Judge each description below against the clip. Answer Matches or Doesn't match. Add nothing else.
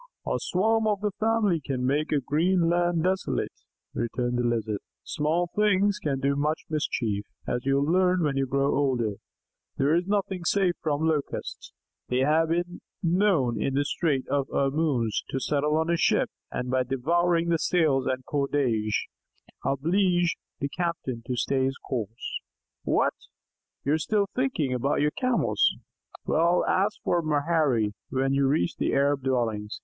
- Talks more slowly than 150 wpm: Doesn't match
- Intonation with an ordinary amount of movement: Matches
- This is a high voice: Doesn't match